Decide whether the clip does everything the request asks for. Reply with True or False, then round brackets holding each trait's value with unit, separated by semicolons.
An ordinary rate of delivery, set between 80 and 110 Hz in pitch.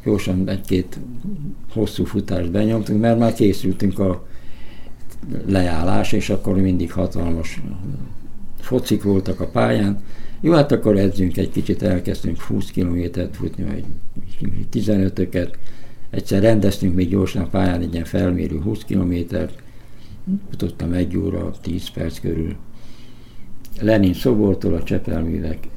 True (120 wpm; 100 Hz)